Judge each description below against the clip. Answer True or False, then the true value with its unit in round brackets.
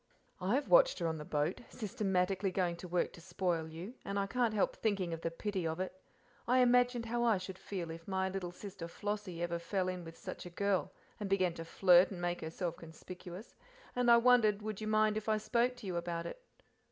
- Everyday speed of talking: False (220 wpm)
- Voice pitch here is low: False (190 Hz)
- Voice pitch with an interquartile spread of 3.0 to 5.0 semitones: True (3.8 semitones)